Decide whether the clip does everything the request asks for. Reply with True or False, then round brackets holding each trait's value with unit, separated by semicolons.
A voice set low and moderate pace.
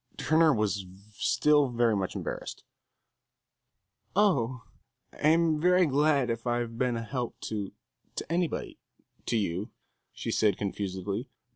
False (120 Hz; 120 wpm)